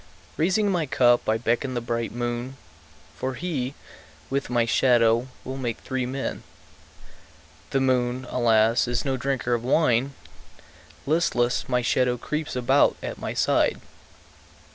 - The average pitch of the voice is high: No, low, 125 Hz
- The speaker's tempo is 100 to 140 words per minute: Yes, slow, 135 wpm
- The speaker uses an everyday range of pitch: No, narrow, 2.0 semitones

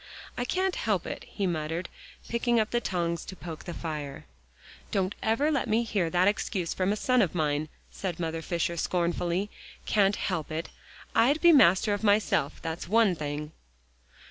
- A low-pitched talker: No, medium, 185 Hz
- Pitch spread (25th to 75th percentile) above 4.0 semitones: Yes, average, 4.8 semitones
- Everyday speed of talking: Yes, average, 170 wpm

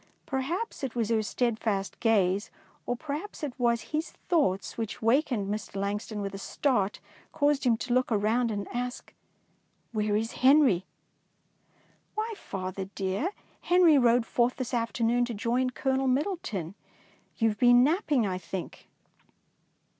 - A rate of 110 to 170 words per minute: Yes, average, 160 wpm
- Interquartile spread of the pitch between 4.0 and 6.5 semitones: Yes, average, 4.4 semitones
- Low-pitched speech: No, high, 235 Hz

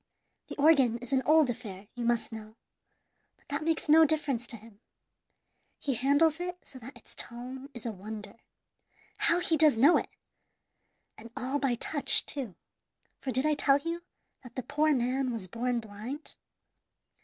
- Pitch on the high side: Yes, very high, 260 Hz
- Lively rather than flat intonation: No, average, 4.2 semitones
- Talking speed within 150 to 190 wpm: Yes, average, 165 wpm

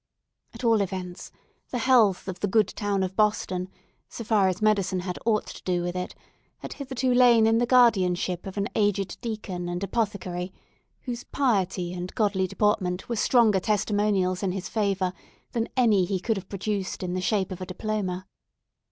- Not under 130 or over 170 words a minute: No, average, 180 wpm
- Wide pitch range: No, average, 3.2 semitones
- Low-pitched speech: No, high, 200 Hz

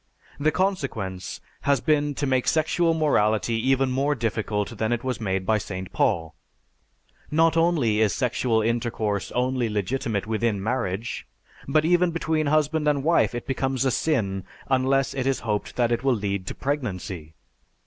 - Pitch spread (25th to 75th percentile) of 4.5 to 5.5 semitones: Yes, average, 5.1 semitones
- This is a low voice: Yes, low, 125 Hz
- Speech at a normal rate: Yes, average, 160 wpm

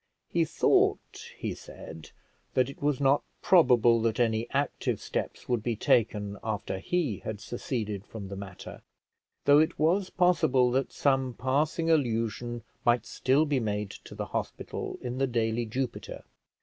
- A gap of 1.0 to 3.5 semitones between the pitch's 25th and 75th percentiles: No, average, 4.1 semitones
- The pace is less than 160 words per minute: Yes, average, 150 wpm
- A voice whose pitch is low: Yes, low, 120 Hz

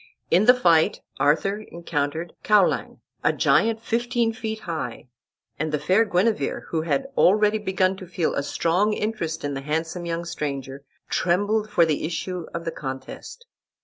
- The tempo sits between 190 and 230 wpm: No, average, 155 wpm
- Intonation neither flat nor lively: Yes, average, 4.9 semitones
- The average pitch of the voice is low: No, medium, 175 Hz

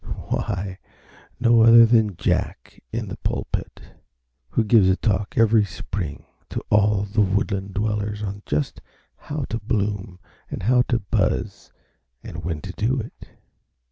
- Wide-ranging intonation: No, average, 2.9 semitones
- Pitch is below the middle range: Yes, low, 105 Hz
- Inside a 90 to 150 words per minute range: Yes, average, 140 wpm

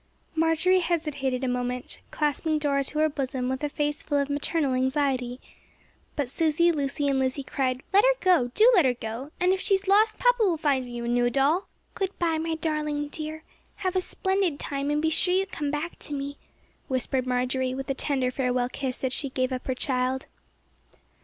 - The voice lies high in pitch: Yes, very high, 285 Hz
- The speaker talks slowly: No, average, 200 wpm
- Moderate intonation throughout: Yes, average, 4.0 semitones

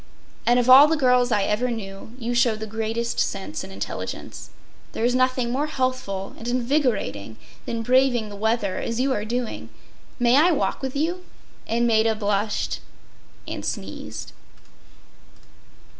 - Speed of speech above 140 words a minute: Yes, average, 150 wpm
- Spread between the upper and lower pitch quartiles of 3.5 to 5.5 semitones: No, average, 2.9 semitones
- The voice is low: No, high, 235 Hz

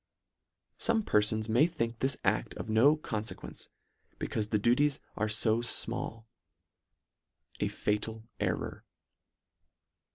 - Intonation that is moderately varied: Yes, average, 3.6 semitones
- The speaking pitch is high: No, low, 115 Hz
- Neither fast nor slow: No, slow, 120 wpm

